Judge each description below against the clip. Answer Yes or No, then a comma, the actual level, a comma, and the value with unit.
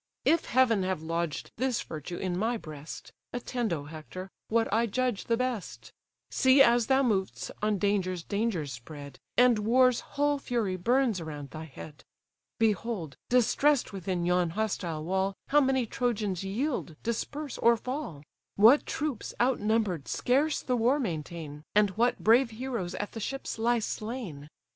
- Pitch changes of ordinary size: No, wide, 5.9 semitones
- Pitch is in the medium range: No, high, 215 Hz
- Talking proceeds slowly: No, average, 155 wpm